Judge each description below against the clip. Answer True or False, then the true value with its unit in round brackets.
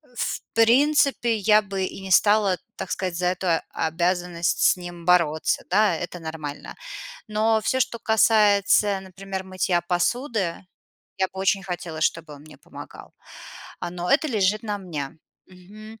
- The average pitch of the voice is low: False (190 Hz)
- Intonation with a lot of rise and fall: False (3.4 semitones)